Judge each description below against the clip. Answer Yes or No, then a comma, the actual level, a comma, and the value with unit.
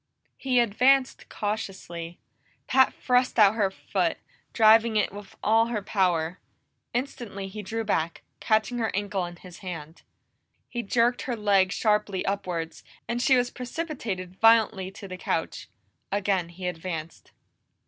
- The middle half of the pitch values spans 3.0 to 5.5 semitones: Yes, average, 4.1 semitones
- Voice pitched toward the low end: No, high, 205 Hz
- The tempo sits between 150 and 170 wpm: No, average, 140 wpm